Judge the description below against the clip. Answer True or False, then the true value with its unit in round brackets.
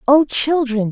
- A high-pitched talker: True (265 Hz)